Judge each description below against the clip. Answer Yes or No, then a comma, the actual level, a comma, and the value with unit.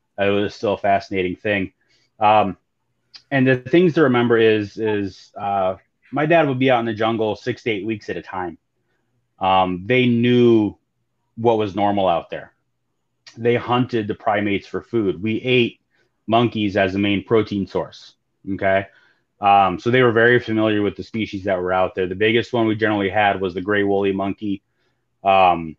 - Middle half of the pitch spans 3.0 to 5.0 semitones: Yes, average, 3.3 semitones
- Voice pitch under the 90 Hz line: No, low, 105 Hz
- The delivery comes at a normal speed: Yes, average, 180 wpm